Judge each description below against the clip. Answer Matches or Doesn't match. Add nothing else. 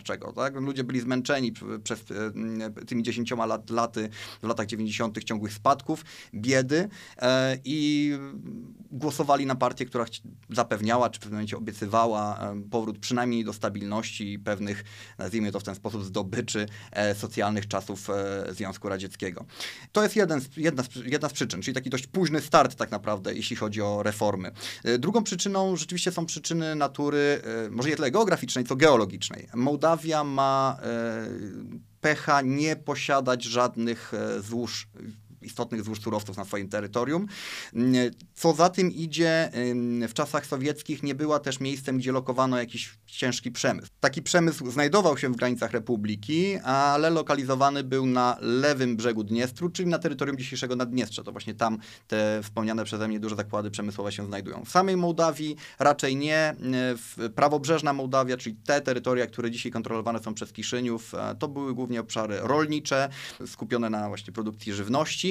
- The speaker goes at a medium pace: Matches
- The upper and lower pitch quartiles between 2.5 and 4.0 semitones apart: Doesn't match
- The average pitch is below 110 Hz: Doesn't match